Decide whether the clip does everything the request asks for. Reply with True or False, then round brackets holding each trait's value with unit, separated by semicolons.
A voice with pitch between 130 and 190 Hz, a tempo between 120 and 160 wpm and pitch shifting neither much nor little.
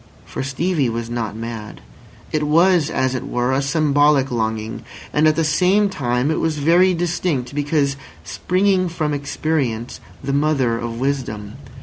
True (140 Hz; 150 wpm; 4.7 semitones)